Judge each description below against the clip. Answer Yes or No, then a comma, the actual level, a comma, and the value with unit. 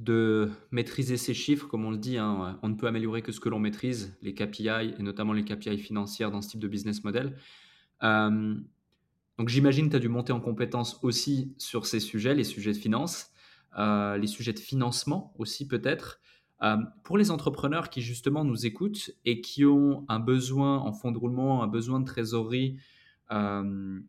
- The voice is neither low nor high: No, low, 115 Hz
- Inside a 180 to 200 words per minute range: Yes, average, 195 wpm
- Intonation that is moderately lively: Yes, average, 3.6 semitones